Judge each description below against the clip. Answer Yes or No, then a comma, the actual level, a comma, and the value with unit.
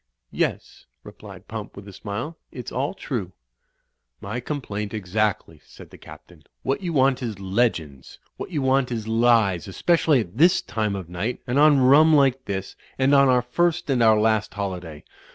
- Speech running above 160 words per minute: Yes, average, 170 wpm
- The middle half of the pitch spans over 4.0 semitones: Yes, wide, 5.4 semitones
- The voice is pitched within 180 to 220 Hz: No, low, 120 Hz